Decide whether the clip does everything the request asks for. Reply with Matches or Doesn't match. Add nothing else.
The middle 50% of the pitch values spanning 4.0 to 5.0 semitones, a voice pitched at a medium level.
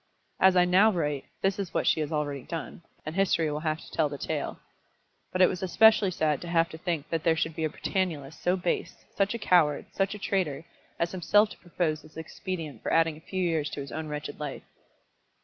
Doesn't match